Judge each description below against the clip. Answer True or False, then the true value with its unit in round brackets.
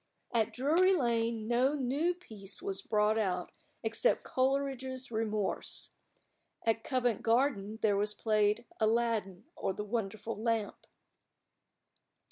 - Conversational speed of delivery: False (110 wpm)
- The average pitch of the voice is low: False (225 Hz)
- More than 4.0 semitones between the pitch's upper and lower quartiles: False (3.5 semitones)